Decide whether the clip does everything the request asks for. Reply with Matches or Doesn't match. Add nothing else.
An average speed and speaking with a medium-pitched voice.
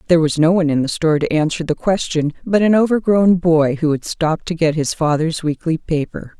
Doesn't match